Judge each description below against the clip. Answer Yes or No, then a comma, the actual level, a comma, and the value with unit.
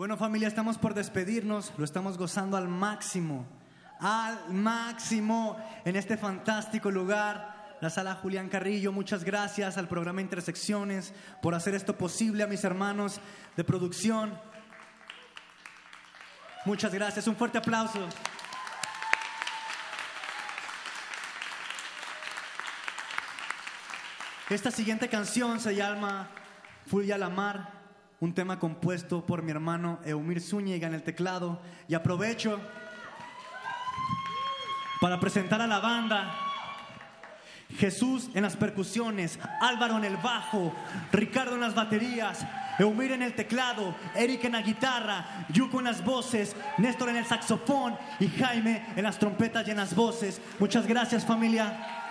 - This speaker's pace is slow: Yes, slow, 120 wpm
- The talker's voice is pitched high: Yes, high, 210 Hz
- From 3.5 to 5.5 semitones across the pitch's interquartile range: No, average, 2.8 semitones